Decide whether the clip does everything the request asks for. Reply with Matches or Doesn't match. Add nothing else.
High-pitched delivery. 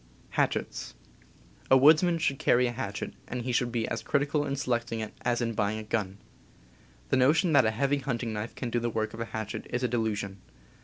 Doesn't match